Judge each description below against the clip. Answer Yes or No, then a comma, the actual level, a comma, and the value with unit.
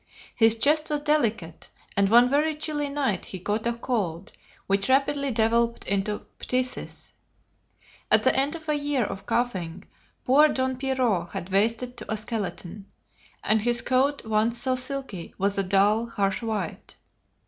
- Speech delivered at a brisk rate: No, average, 155 wpm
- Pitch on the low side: No, high, 235 Hz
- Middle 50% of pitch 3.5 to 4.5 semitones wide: No, average, 5.0 semitones